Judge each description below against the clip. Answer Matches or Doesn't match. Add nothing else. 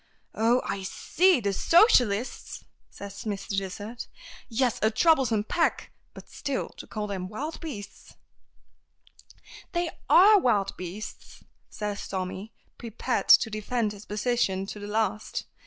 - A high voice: Matches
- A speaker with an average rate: Doesn't match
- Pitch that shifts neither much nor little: Matches